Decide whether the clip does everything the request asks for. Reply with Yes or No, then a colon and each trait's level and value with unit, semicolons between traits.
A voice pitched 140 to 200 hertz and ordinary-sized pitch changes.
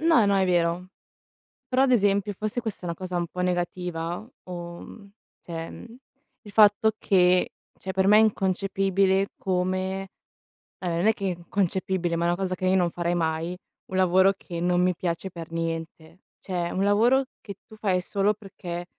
No: medium, 185 Hz; narrow, 2.3 semitones